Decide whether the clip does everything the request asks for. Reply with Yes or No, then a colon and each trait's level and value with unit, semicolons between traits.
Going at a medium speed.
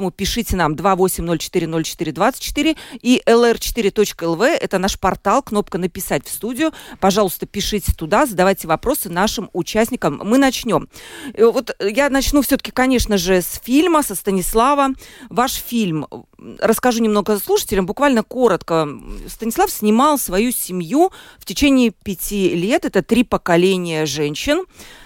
Yes: average, 120 wpm